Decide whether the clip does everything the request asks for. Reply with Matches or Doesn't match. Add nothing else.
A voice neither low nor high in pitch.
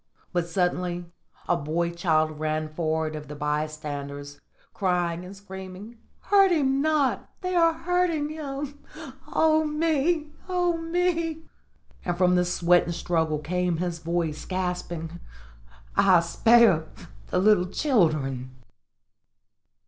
Matches